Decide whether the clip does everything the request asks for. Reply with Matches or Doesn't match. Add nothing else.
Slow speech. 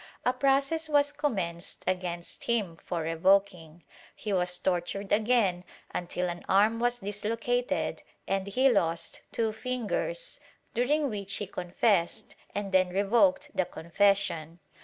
Matches